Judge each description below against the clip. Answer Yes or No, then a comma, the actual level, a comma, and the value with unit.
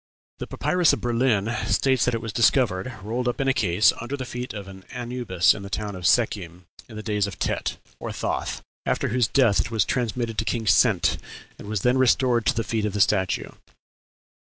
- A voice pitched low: Yes, low, 115 Hz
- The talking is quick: Yes, fast, 210 wpm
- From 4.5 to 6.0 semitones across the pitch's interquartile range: No, average, 3.3 semitones